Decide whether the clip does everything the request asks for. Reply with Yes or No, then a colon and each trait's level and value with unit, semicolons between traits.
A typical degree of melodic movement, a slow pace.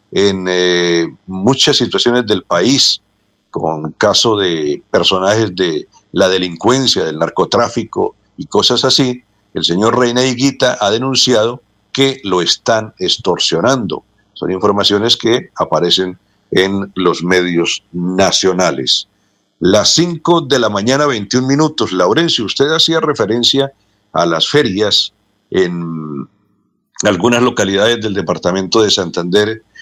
No: wide, 6.1 semitones; slow, 115 wpm